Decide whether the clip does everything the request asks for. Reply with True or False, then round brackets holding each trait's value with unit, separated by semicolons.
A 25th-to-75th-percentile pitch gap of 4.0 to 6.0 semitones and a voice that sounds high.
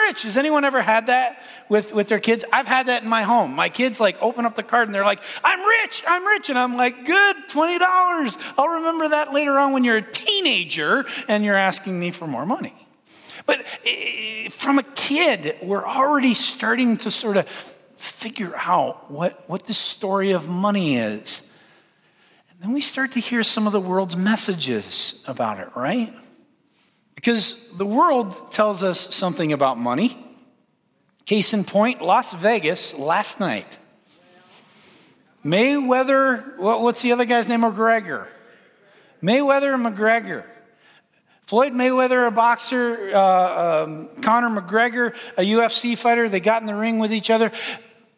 True (4.3 semitones; 235 Hz)